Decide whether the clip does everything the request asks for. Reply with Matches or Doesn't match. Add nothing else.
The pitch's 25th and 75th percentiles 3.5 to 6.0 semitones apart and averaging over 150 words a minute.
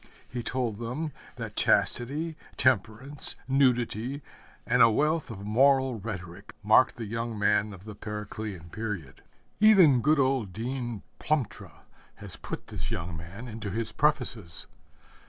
Doesn't match